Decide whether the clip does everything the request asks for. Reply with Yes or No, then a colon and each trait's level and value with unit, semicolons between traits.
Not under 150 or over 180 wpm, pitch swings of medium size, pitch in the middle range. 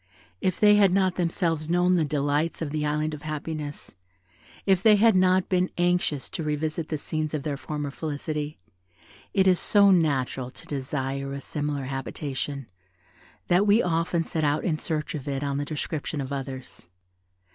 Yes: average, 170 wpm; average, 3.6 semitones; medium, 155 Hz